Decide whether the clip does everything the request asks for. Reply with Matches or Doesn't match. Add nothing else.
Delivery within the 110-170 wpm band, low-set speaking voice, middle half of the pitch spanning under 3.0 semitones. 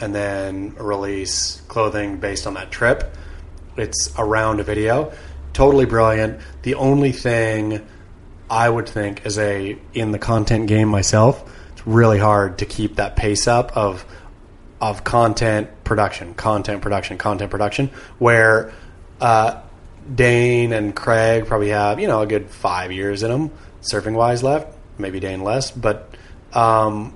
Matches